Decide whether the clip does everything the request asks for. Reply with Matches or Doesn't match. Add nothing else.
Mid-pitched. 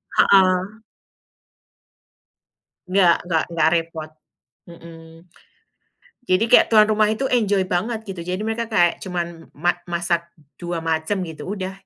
Matches